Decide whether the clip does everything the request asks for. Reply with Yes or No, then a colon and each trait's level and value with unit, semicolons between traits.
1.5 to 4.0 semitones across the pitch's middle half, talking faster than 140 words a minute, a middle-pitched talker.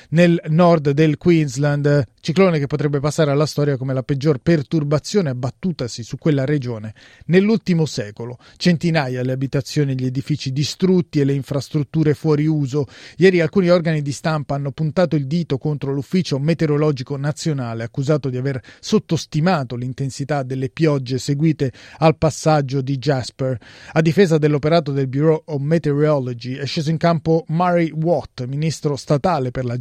Yes: average, 2.8 semitones; average, 150 wpm; medium, 150 Hz